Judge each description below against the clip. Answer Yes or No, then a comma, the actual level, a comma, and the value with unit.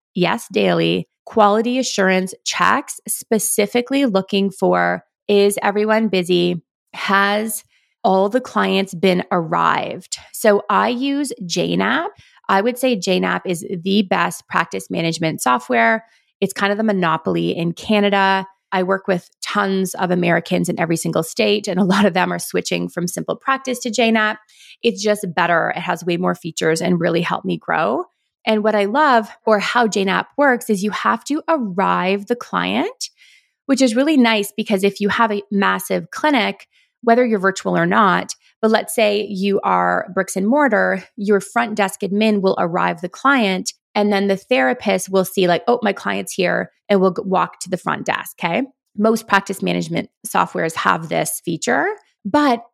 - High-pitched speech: Yes, high, 200 Hz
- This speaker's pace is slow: No, average, 165 wpm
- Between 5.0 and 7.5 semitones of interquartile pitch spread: No, average, 3.7 semitones